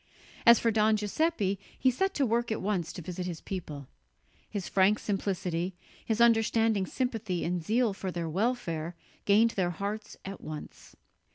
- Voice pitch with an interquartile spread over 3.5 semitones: Yes, average, 4.1 semitones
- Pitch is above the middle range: Yes, high, 200 Hz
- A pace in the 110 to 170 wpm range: Yes, average, 160 wpm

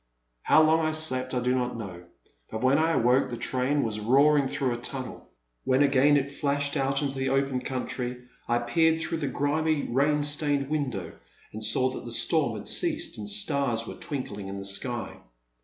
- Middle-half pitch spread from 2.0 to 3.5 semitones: Yes, average, 3.2 semitones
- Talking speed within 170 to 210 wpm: Yes, average, 190 wpm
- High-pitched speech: No, low, 130 Hz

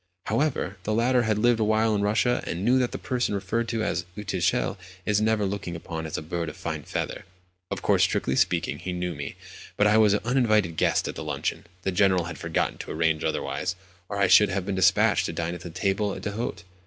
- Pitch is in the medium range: No, low, 100 Hz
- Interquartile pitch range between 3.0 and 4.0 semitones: Yes, average, 3.7 semitones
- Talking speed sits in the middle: No, fast, 220 wpm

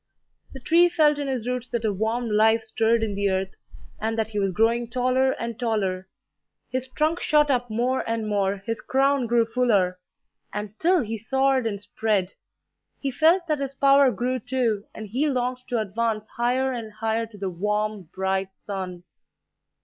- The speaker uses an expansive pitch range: No, average, 3.7 semitones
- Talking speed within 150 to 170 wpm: No, average, 180 wpm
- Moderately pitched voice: No, high, 230 Hz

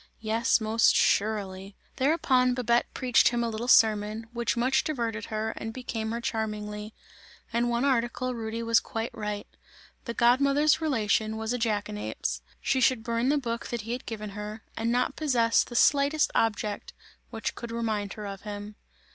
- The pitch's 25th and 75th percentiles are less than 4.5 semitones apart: Yes, narrow, 2.4 semitones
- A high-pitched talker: Yes, high, 230 Hz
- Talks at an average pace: Yes, average, 170 wpm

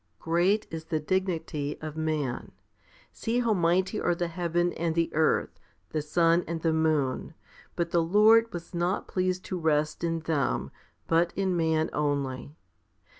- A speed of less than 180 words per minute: Yes, average, 155 wpm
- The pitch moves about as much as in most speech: No, narrow, 2.2 semitones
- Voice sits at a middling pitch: Yes, medium, 165 Hz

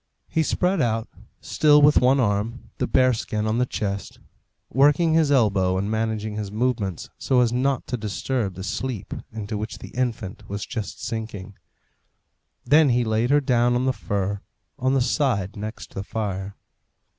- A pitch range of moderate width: Yes, average, 4.0 semitones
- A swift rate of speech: No, average, 170 wpm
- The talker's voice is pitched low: Yes, low, 115 Hz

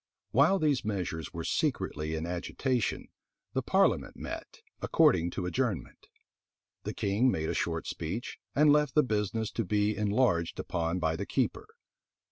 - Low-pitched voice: Yes, low, 105 Hz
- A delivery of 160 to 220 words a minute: No, average, 145 wpm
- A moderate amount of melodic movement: No, wide, 7.2 semitones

